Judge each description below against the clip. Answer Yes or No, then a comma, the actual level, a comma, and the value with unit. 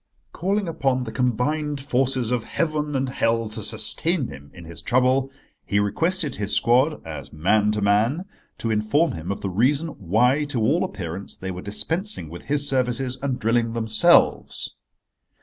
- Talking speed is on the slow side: No, average, 165 wpm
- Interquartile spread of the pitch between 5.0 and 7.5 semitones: Yes, wide, 5.5 semitones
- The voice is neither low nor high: No, low, 125 Hz